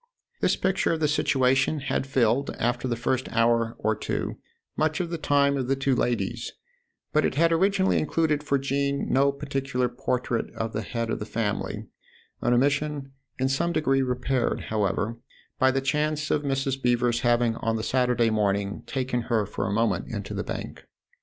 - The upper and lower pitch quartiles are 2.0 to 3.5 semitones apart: Yes, average, 3.2 semitones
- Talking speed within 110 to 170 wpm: No, average, 180 wpm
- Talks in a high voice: No, low, 130 Hz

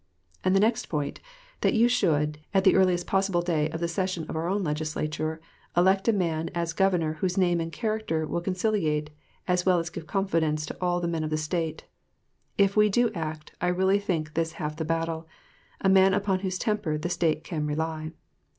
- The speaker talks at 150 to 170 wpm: No, average, 200 wpm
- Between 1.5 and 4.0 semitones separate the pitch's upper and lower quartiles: Yes, average, 3.4 semitones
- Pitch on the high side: No, medium, 170 Hz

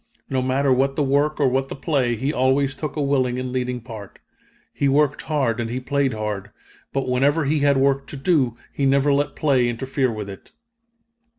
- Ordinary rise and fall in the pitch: No, narrow, 2.0 semitones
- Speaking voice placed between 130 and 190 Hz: Yes, low, 135 Hz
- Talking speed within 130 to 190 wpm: No, average, 200 wpm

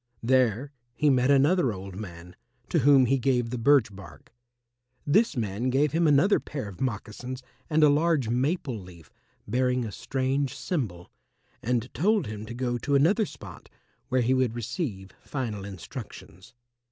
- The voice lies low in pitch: Yes, low, 125 Hz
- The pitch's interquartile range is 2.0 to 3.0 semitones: No, average, 4.9 semitones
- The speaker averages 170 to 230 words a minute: No, average, 155 wpm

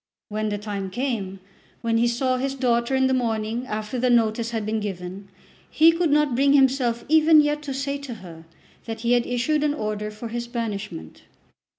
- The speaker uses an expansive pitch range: No, average, 4.0 semitones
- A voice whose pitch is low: No, high, 235 Hz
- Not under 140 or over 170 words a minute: No, average, 195 wpm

